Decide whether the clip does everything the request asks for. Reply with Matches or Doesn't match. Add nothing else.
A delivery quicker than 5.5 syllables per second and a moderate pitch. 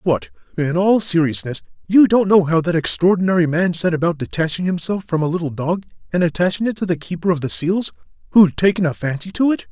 Matches